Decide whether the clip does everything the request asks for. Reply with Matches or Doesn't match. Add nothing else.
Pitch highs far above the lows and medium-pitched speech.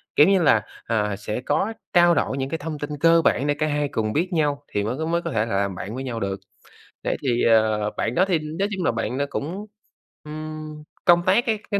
Matches